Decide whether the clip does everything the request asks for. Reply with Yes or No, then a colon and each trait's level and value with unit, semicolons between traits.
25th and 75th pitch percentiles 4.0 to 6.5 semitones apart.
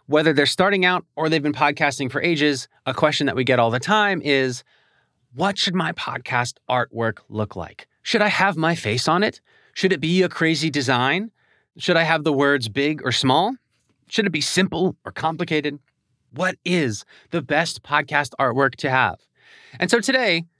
Yes: average, 5.2 semitones